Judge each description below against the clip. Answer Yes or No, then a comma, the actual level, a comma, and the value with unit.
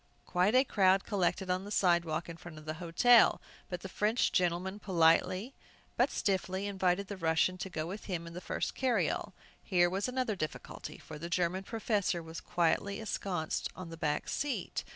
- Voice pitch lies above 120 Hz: Yes, medium, 185 Hz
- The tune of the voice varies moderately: Yes, average, 3.0 semitones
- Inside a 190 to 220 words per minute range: No, average, 180 wpm